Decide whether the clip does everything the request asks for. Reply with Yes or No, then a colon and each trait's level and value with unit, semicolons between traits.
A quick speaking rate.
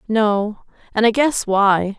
No: average, 150 wpm